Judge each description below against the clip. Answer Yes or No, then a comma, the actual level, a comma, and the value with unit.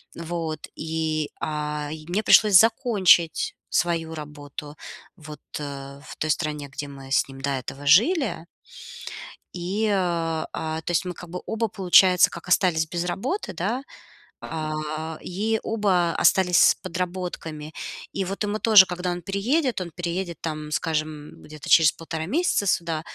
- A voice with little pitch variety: No, average, 3.5 semitones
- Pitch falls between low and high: Yes, medium, 170 Hz